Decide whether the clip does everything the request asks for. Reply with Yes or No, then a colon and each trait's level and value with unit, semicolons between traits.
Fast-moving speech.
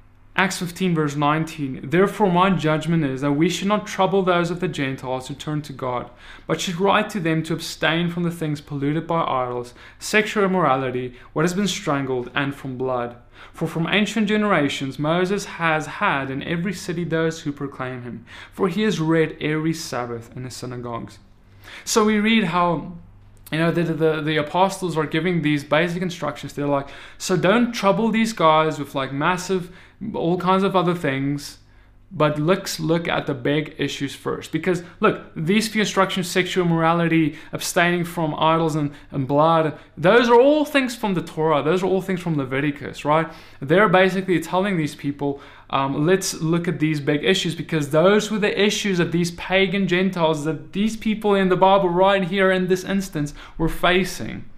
No: average, 180 wpm